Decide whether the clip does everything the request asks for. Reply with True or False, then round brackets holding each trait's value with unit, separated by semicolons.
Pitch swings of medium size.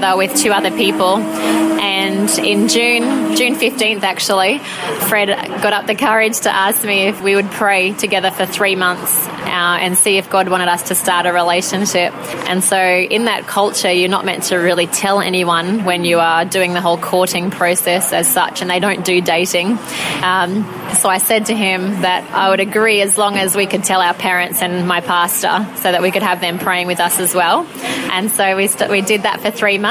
False (2.2 semitones)